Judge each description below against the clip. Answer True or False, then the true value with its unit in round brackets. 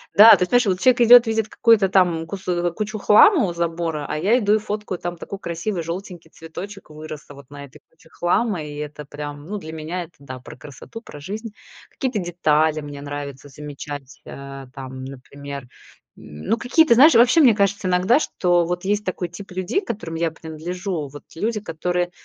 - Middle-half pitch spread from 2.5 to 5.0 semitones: False (5.6 semitones)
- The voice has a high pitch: False (175 Hz)